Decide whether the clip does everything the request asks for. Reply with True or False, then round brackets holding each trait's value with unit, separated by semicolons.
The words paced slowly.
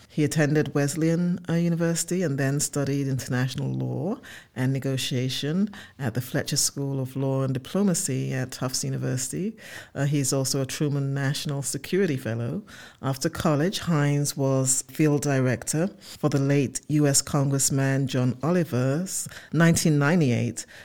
True (130 wpm)